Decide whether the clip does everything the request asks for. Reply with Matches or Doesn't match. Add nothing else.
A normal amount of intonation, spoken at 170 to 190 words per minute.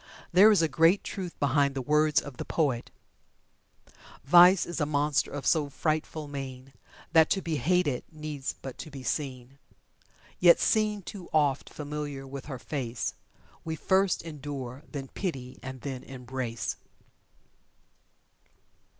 Doesn't match